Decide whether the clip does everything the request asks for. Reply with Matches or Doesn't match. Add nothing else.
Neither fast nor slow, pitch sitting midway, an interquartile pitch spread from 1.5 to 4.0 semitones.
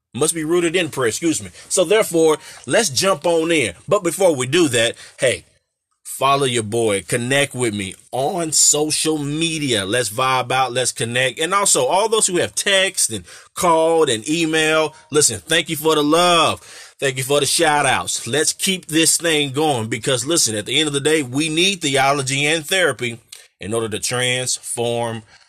Doesn't match